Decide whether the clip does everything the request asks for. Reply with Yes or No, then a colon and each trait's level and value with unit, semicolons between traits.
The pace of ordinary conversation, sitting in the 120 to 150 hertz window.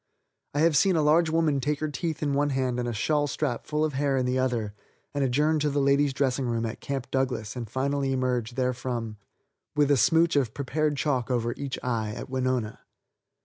No: fast, 210 wpm; low, 135 Hz